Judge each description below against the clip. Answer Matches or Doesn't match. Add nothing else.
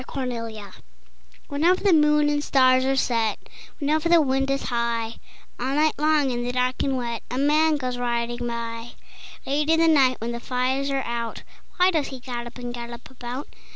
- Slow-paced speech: Doesn't match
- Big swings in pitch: Doesn't match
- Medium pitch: Doesn't match